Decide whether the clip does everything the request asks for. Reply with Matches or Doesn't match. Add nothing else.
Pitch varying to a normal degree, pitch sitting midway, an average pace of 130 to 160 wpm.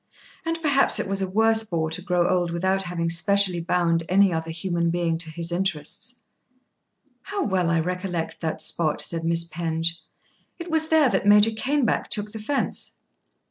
Doesn't match